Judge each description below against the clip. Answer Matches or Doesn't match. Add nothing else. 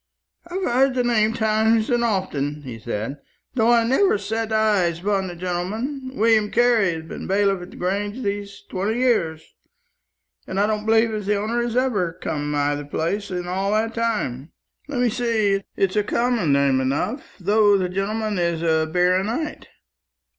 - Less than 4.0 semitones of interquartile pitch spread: Doesn't match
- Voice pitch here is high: Matches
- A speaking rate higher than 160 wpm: Matches